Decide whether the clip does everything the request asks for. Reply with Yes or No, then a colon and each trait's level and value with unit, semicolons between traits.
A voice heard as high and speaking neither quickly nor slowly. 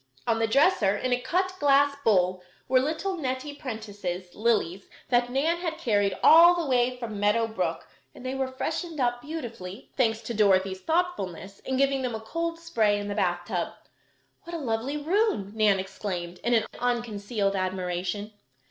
Yes: high, 235 Hz; average, 165 wpm